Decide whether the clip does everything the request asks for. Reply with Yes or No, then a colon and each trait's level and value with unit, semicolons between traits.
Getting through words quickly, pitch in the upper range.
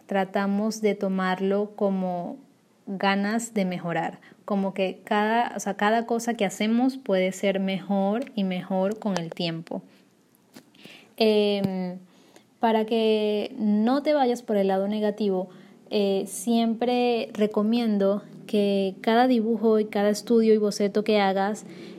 No: average, 130 wpm; high, 205 Hz